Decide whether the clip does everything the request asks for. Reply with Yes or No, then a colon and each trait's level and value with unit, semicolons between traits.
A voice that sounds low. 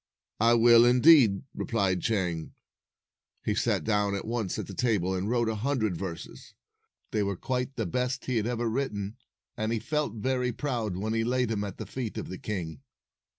Yes: low, 110 Hz